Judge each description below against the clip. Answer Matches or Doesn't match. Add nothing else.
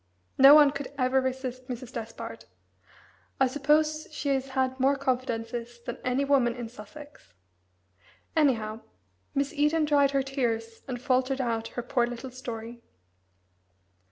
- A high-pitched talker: Matches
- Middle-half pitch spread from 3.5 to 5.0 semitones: Doesn't match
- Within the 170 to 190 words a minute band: Doesn't match